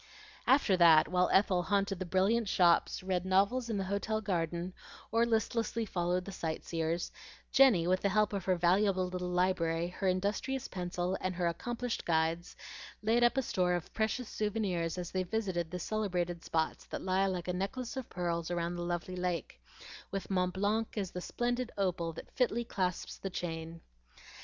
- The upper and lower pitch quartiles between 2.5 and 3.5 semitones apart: Yes, average, 3.1 semitones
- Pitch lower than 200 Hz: Yes, medium, 185 Hz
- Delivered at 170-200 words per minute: Yes, average, 175 wpm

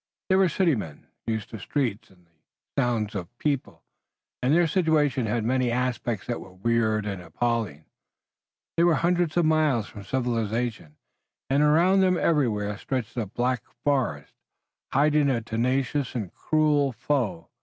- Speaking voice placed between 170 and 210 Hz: No, low, 125 Hz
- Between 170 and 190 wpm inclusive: No, average, 155 wpm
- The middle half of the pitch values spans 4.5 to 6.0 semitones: Yes, wide, 5.5 semitones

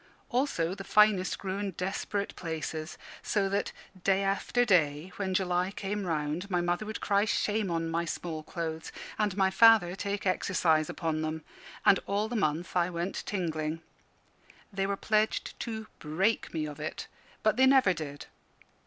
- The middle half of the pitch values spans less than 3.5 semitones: No, average, 3.8 semitones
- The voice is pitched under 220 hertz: Yes, medium, 185 Hz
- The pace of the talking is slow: No, average, 160 wpm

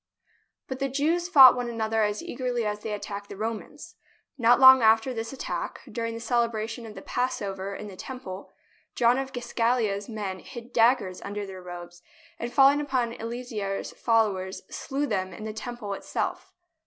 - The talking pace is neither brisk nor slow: Yes, average, 170 wpm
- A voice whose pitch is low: No, high, 230 Hz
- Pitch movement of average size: Yes, average, 3.4 semitones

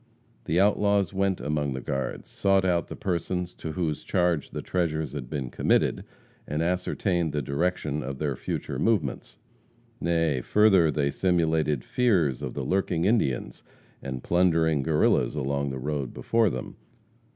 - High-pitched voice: No, very low, 80 Hz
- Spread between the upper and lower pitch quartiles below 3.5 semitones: No, average, 4.3 semitones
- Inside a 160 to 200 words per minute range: No, average, 150 wpm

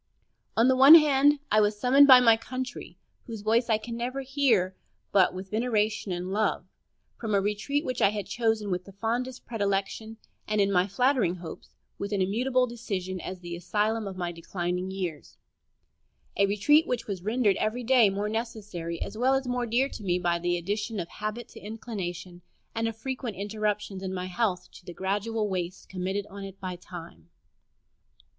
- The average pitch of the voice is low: No, high, 210 Hz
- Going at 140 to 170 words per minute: No, average, 185 wpm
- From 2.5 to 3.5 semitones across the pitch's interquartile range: No, average, 4.1 semitones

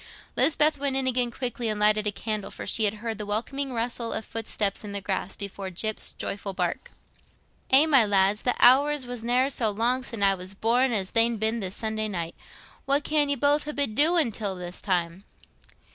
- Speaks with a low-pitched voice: No, high, 225 Hz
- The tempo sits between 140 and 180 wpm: No, fast, 205 wpm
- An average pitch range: Yes, average, 4.4 semitones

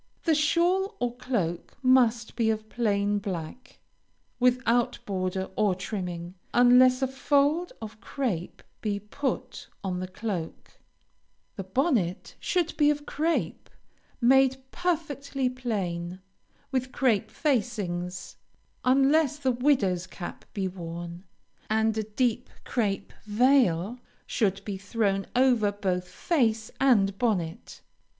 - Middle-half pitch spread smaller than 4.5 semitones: No, wide, 5.4 semitones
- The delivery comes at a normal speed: No, slow, 115 wpm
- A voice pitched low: No, high, 225 Hz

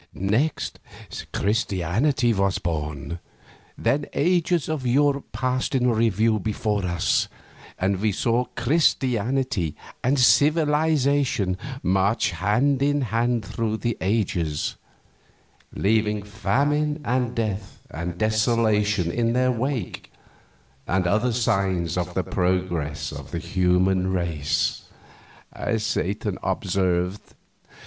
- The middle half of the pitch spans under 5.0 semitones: No, wide, 5.5 semitones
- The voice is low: Yes, low, 110 Hz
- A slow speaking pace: Yes, slow, 105 wpm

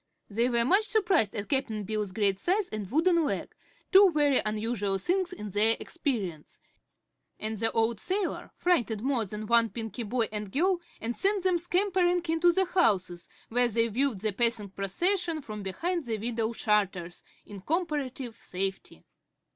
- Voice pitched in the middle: No, high, 235 Hz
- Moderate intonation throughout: No, wide, 8.5 semitones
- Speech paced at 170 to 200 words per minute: No, average, 160 wpm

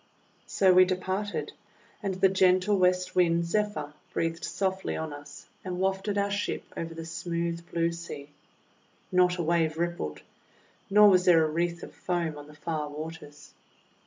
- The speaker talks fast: No, average, 160 wpm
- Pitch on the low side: No, medium, 175 Hz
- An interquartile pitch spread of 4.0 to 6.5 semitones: No, narrow, 2.4 semitones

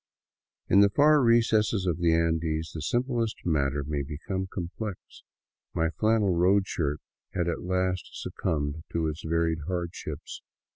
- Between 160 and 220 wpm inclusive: No, average, 140 wpm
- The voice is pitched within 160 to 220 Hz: No, very low, 85 Hz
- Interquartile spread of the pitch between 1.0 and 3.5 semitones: No, average, 3.9 semitones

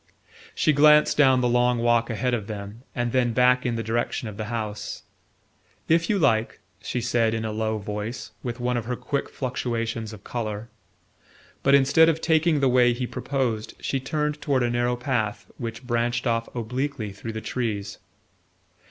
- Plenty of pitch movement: No, average, 2.7 semitones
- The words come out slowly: No, average, 180 wpm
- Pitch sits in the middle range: No, low, 120 Hz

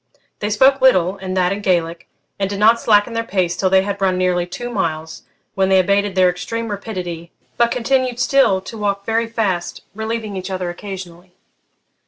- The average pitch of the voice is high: Yes, high, 195 Hz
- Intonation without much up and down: No, average, 3.6 semitones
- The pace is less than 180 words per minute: No, average, 185 wpm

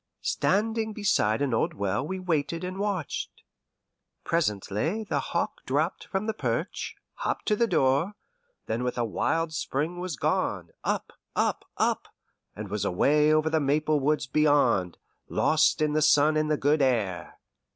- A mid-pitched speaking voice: Yes, medium, 150 Hz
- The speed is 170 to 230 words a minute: No, average, 155 wpm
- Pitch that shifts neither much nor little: No, wide, 5.9 semitones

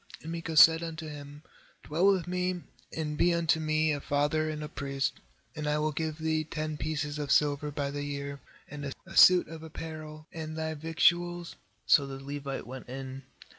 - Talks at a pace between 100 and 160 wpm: No, average, 185 wpm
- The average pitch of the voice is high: No, medium, 155 Hz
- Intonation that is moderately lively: No, narrow, 2.0 semitones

